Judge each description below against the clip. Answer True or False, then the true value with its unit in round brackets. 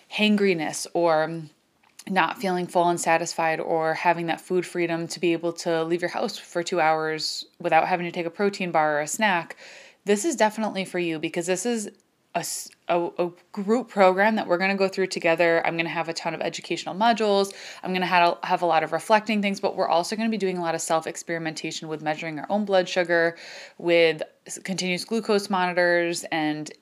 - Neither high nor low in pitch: True (175 Hz)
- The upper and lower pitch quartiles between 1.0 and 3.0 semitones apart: True (2.7 semitones)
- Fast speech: True (210 wpm)